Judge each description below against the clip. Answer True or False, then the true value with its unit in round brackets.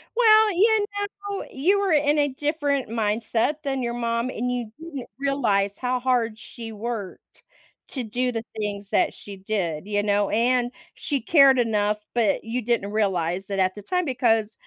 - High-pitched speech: True (235 Hz)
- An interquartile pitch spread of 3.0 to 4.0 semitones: False (4.9 semitones)